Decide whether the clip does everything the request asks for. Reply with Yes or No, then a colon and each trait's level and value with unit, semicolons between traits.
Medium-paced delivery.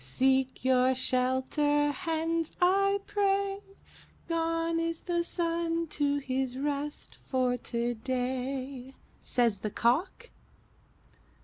No: slow, 95 wpm